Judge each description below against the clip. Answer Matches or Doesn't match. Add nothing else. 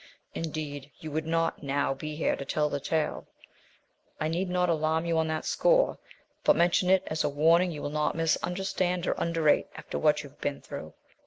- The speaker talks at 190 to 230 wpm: Matches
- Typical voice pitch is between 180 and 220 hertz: Doesn't match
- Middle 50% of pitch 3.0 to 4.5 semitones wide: Doesn't match